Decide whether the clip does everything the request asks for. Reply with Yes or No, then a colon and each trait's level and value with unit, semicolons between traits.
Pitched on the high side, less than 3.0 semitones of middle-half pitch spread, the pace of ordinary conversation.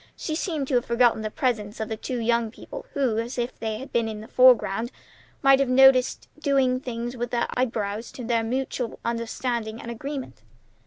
Yes: high, 240 Hz; narrow, 2.4 semitones; average, 195 wpm